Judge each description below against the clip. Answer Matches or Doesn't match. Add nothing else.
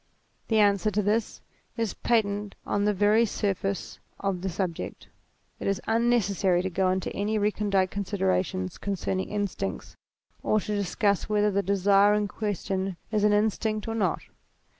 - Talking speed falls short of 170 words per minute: Matches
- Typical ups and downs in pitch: Doesn't match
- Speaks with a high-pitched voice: Matches